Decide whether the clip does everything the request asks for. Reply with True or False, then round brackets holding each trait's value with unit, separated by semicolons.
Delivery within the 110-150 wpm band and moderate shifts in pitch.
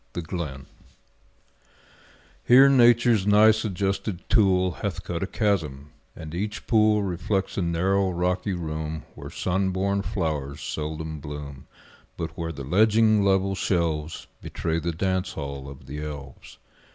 True (135 wpm; 4.3 semitones)